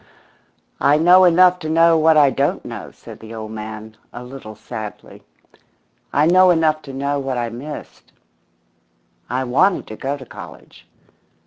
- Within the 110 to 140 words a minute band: No, average, 155 wpm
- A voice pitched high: No, medium, 140 Hz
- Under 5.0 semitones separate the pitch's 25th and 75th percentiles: No, average, 5.3 semitones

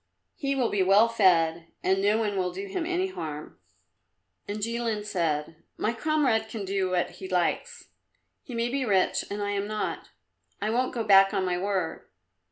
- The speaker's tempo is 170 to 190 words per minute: Yes, average, 180 wpm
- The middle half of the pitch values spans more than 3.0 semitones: Yes, average, 3.7 semitones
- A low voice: No, high, 205 Hz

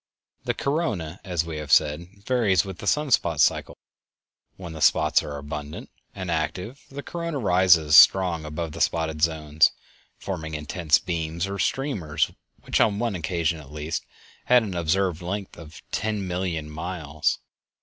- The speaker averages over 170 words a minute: No, average, 155 wpm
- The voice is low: Yes, very low, 85 Hz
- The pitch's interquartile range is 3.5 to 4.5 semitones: Yes, average, 4.1 semitones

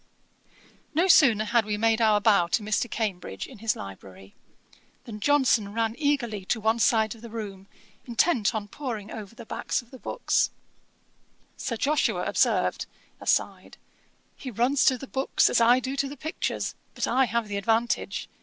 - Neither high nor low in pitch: No, high, 230 Hz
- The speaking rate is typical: Yes, average, 170 wpm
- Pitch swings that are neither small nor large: Yes, average, 3.5 semitones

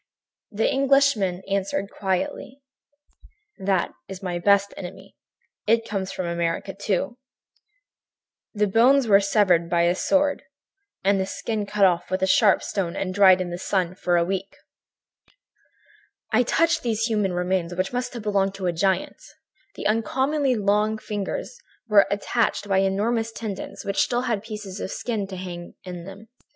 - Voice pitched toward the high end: Yes, high, 200 Hz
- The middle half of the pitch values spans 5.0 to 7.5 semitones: No, average, 3.1 semitones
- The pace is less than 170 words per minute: Yes, average, 160 wpm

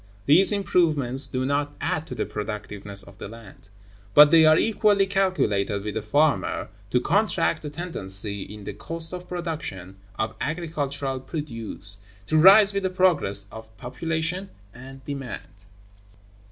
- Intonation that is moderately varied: No, wide, 7.9 semitones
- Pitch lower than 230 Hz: Yes, medium, 140 Hz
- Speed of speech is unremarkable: Yes, average, 145 wpm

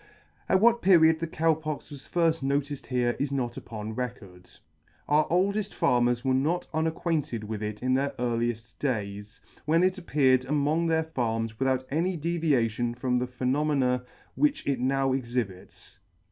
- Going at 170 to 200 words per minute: No, average, 155 wpm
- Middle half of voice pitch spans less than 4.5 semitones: No, average, 4.8 semitones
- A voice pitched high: No, low, 135 Hz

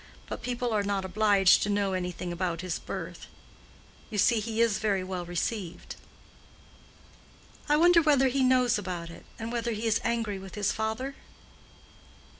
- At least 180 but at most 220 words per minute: No, average, 160 wpm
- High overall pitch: Yes, high, 210 Hz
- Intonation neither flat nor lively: Yes, average, 4.0 semitones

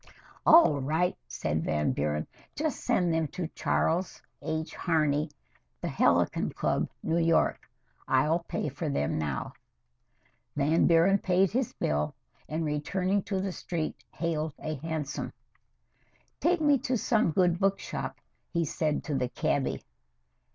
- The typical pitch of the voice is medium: Yes, medium, 160 Hz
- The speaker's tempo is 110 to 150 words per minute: Yes, slow, 135 wpm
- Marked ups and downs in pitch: No, average, 4.1 semitones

